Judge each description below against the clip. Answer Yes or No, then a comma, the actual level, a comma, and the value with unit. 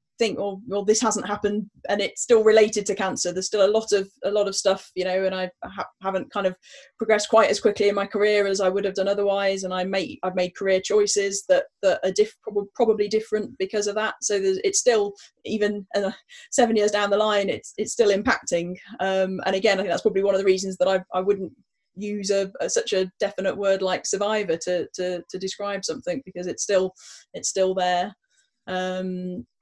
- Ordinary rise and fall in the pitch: No, narrow, 2.3 semitones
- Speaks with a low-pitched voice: No, high, 200 Hz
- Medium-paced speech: No, fast, 225 wpm